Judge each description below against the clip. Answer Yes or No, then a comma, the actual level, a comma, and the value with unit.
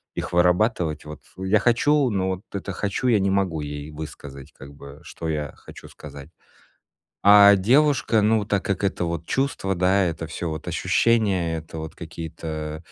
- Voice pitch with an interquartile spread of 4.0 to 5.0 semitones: Yes, average, 4.6 semitones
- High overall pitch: No, very low, 90 Hz